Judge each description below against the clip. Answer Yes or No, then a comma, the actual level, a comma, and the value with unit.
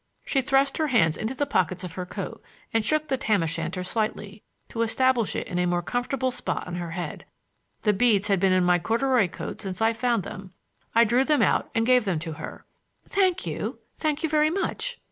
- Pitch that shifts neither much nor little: No, wide, 6.4 semitones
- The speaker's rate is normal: No, fast, 220 wpm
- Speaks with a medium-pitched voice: No, high, 225 Hz